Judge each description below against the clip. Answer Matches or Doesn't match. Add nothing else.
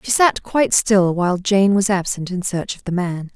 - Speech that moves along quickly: Matches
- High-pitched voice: Matches